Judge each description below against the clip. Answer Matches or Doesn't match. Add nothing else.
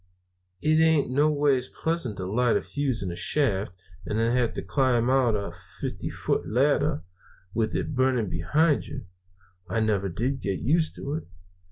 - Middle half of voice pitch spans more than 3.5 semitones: Matches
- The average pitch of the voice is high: Doesn't match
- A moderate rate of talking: Matches